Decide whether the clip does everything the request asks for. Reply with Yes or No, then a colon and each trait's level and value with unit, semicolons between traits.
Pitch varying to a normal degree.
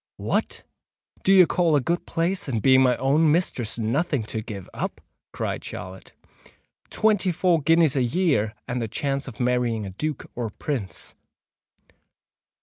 No: wide, 6.4 semitones